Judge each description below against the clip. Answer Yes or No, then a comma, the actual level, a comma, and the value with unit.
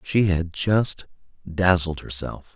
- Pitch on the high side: No, very low, 90 Hz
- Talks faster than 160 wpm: No, slow, 120 wpm